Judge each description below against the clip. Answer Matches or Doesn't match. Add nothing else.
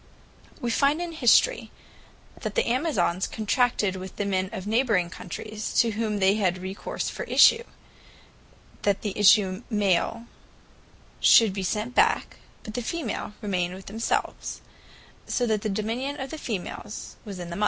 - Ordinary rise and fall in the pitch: Matches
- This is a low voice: Doesn't match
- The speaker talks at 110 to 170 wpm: Matches